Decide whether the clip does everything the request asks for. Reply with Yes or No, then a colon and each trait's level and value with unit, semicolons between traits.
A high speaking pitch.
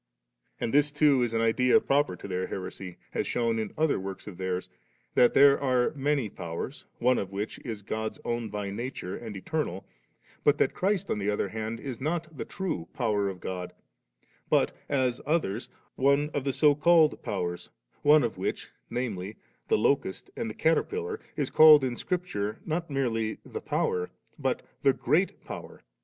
No: low, 120 Hz